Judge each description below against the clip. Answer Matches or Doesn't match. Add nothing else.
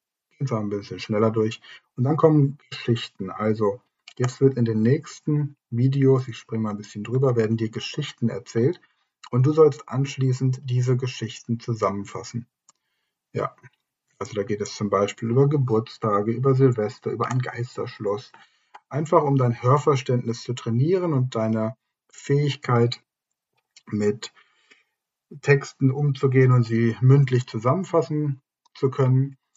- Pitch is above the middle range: Doesn't match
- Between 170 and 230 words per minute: Doesn't match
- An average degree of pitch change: Matches